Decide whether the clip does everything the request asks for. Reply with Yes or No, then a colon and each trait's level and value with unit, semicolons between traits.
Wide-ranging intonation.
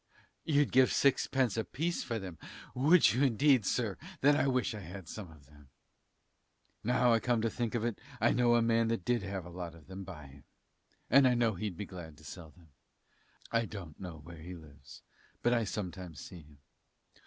Yes: wide, 6.0 semitones